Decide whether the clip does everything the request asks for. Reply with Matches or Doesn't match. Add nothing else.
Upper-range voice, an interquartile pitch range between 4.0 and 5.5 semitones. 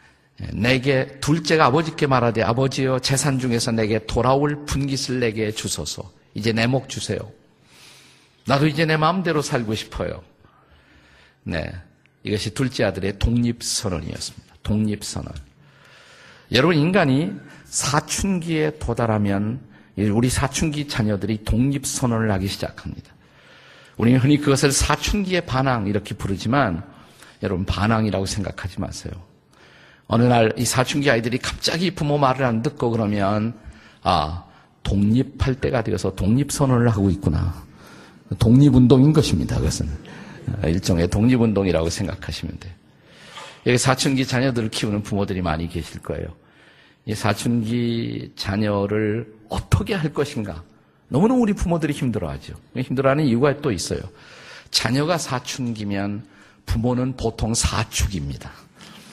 Doesn't match